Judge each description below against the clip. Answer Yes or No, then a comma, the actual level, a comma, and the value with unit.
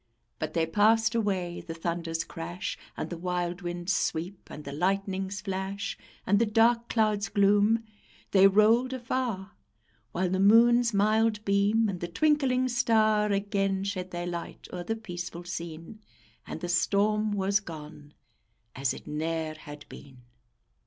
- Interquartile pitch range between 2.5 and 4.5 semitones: Yes, average, 3.7 semitones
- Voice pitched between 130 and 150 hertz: No, high, 195 Hz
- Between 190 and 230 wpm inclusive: No, average, 145 wpm